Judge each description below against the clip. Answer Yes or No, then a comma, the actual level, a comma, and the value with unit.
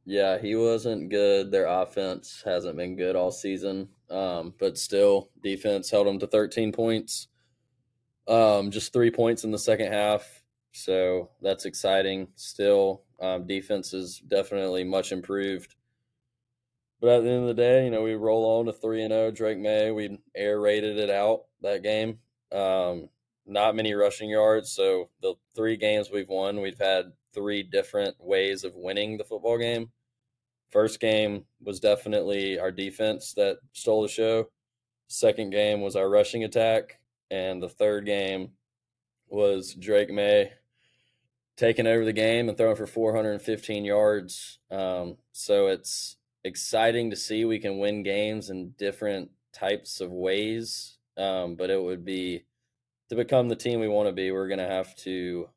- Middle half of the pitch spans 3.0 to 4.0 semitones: Yes, average, 3.3 semitones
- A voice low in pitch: Yes, low, 105 Hz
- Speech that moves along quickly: No, average, 160 wpm